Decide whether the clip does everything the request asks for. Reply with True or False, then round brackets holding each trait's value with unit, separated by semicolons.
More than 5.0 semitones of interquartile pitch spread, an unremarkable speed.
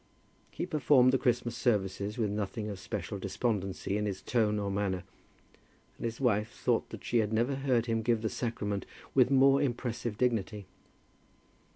False (3.2 semitones; 165 wpm)